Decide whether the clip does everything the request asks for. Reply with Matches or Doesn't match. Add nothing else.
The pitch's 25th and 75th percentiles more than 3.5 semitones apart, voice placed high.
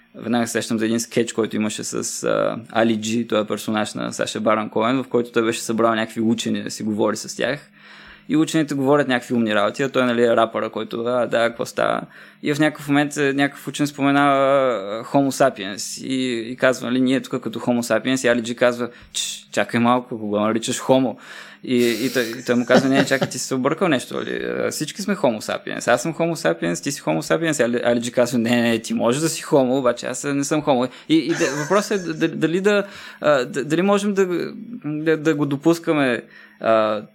Doesn't match